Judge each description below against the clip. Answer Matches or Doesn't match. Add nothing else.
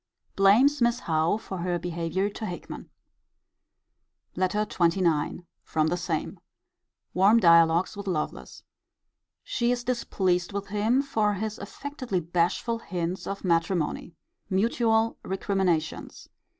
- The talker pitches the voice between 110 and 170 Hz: Doesn't match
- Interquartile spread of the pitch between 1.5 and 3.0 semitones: Doesn't match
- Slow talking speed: Matches